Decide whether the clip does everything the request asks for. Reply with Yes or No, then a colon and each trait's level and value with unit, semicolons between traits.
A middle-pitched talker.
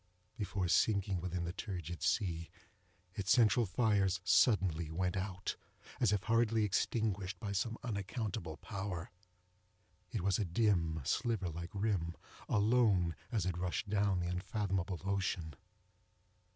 No: very low, 95 Hz